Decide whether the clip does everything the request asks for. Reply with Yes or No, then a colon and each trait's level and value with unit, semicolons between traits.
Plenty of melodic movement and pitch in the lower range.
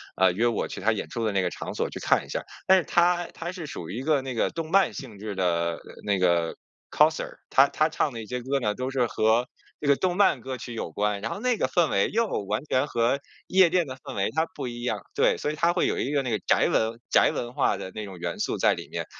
Yes: wide, 7.0 semitones; low, 125 Hz